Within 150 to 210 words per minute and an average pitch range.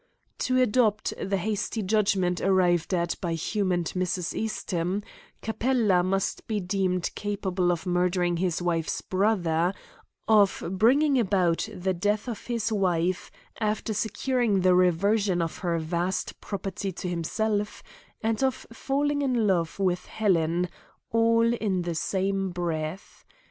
No: slow, 135 wpm; average, 3.5 semitones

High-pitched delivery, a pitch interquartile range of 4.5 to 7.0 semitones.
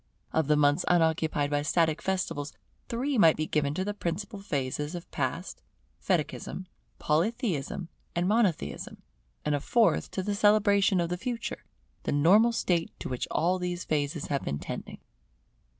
No: medium, 170 Hz; average, 5.2 semitones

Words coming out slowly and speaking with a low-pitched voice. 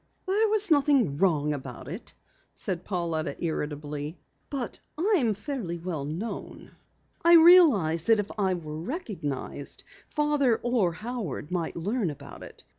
No: slow, 130 wpm; high, 190 Hz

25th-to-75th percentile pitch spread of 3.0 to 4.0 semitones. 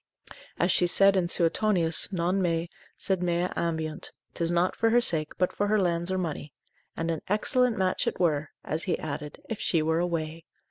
No: narrow, 2.5 semitones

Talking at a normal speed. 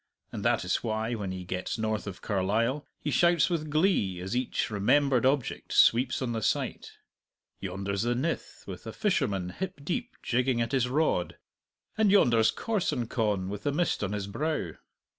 Yes: average, 170 wpm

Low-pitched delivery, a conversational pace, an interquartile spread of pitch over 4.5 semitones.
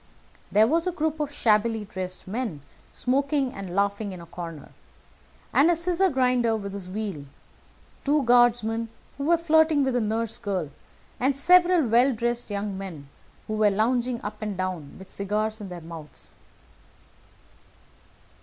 No: high, 225 Hz; average, 150 wpm; wide, 5.4 semitones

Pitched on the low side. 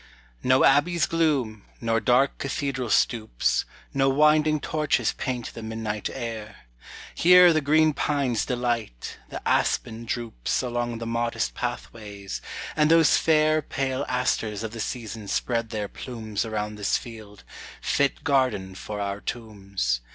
Yes: low, 120 Hz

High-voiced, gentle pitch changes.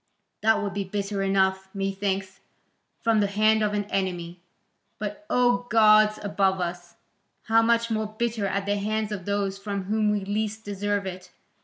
Yes: high, 205 Hz; narrow, 1.9 semitones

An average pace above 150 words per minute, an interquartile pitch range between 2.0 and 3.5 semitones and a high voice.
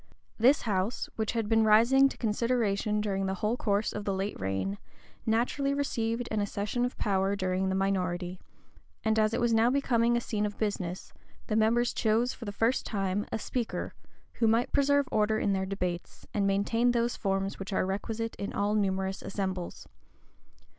Yes: average, 180 wpm; average, 3.1 semitones; high, 210 Hz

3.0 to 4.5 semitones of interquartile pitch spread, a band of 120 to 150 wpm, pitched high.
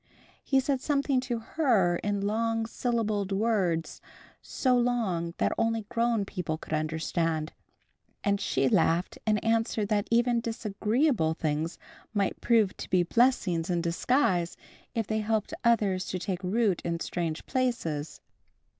No: average, 5.1 semitones; slow, 135 wpm; high, 205 Hz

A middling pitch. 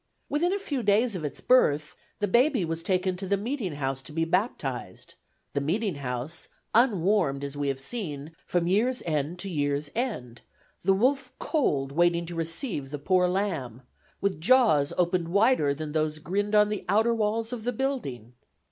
Yes: medium, 180 Hz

